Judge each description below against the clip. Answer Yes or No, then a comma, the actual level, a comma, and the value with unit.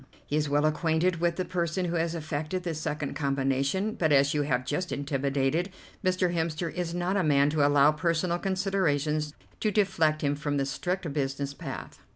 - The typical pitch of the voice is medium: Yes, medium, 155 Hz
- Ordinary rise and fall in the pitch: Yes, average, 3.5 semitones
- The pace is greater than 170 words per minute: Yes, average, 185 wpm